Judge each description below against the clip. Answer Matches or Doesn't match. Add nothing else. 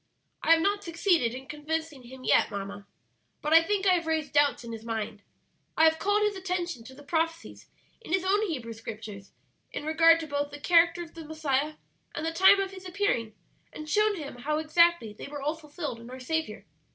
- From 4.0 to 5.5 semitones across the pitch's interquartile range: Matches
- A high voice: Matches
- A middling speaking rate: Doesn't match